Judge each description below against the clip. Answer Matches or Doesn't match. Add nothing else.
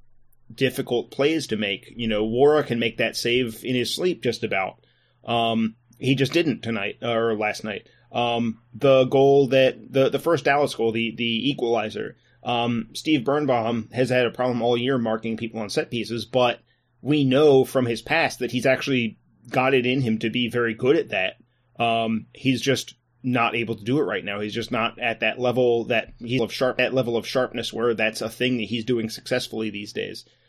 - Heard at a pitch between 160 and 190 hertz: Doesn't match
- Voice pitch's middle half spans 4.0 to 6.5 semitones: Doesn't match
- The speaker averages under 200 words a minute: Doesn't match